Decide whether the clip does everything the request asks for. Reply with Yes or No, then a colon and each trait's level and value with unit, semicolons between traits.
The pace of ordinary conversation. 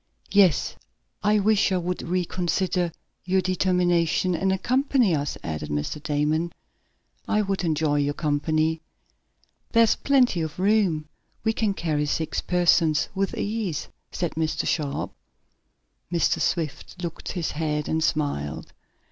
No: slow, 125 wpm